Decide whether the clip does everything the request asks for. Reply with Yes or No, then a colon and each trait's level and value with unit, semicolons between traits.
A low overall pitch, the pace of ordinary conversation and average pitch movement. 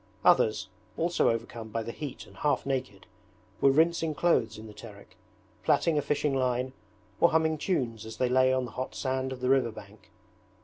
Yes: low, 130 Hz; average, 185 wpm; average, 4.4 semitones